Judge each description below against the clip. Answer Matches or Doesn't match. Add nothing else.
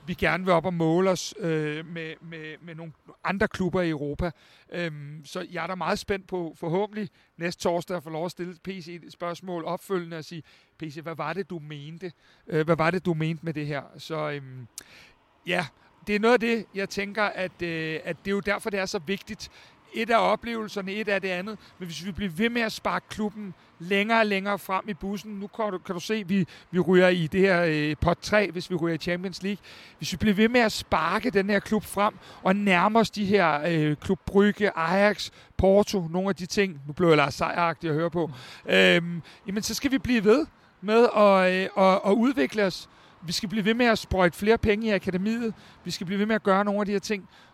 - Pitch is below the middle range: Doesn't match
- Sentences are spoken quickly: Matches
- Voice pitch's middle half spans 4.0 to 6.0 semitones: Doesn't match